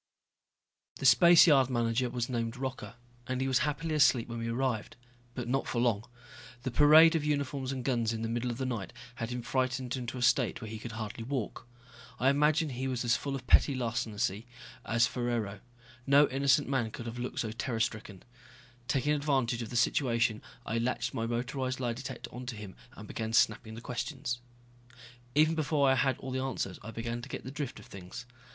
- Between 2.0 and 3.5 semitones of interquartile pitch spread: Yes, average, 2.7 semitones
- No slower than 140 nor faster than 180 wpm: No, average, 200 wpm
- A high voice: No, low, 125 Hz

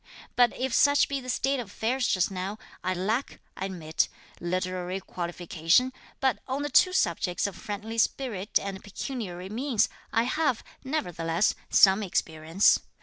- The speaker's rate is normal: Yes, average, 145 wpm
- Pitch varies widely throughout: Yes, wide, 5.7 semitones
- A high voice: Yes, high, 205 Hz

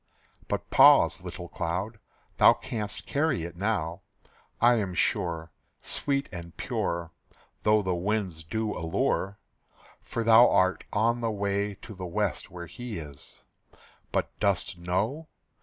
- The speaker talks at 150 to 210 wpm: No, slow, 135 wpm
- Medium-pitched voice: No, low, 100 Hz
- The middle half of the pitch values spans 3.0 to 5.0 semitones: Yes, average, 4.4 semitones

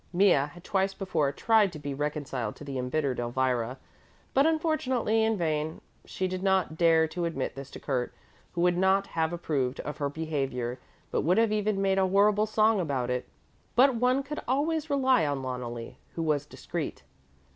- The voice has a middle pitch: Yes, medium, 170 Hz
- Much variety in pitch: Yes, wide, 7.3 semitones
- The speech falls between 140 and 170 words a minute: No, average, 180 wpm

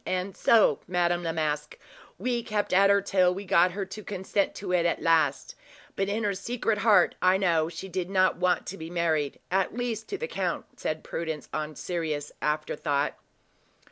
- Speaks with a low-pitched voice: No, medium, 185 Hz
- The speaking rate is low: No, average, 180 wpm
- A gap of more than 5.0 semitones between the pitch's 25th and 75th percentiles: No, average, 3.6 semitones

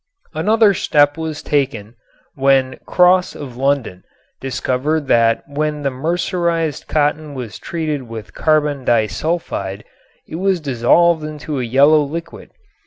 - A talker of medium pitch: Yes, medium, 145 Hz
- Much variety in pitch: No, average, 3.7 semitones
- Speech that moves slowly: Yes, slow, 120 wpm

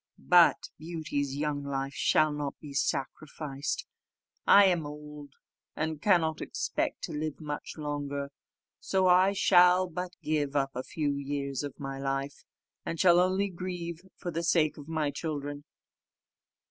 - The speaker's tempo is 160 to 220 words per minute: No, average, 145 wpm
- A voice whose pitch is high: No, medium, 150 Hz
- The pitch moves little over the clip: No, average, 3.4 semitones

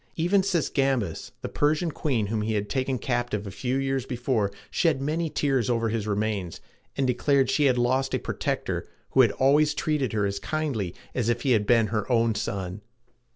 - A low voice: Yes, low, 125 Hz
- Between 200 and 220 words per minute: No, average, 190 wpm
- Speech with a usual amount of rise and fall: Yes, average, 4.4 semitones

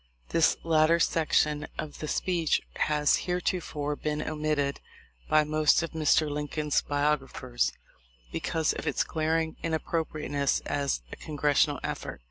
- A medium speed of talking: No, slow, 130 wpm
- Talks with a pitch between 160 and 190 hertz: No, medium, 150 Hz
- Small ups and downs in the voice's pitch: Yes, narrow, 1.6 semitones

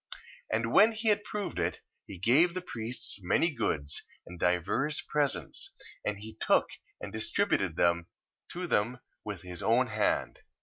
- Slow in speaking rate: No, average, 150 wpm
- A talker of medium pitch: No, low, 110 Hz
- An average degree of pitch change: No, wide, 9.0 semitones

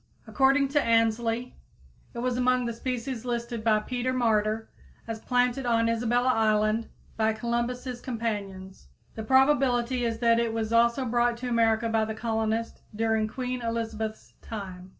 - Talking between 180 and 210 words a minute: No, average, 150 wpm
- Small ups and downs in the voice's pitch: Yes, narrow, 1.9 semitones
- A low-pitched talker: No, high, 230 Hz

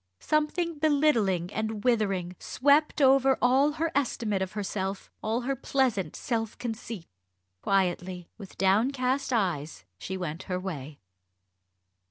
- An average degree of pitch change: No, wide, 6.1 semitones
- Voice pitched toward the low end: No, high, 220 Hz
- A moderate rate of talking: No, slow, 120 wpm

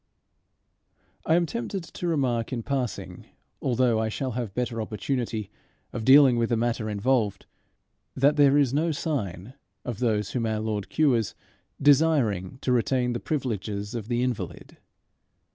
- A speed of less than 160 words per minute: Yes, average, 145 wpm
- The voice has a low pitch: Yes, low, 120 Hz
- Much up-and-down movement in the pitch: No, average, 3.7 semitones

